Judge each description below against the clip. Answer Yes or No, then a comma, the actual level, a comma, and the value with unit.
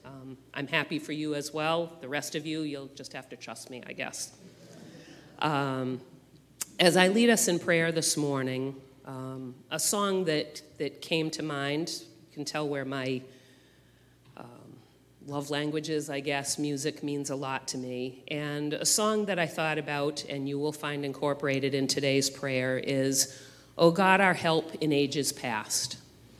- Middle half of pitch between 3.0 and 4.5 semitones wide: No, narrow, 2.6 semitones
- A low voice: No, medium, 145 Hz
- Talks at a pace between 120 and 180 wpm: Yes, average, 170 wpm